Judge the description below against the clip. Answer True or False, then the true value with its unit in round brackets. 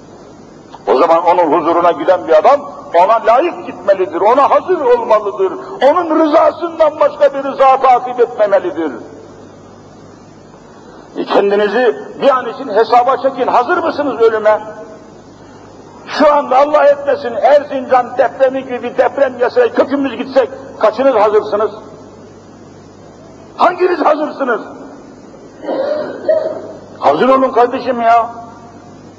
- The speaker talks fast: False (100 wpm)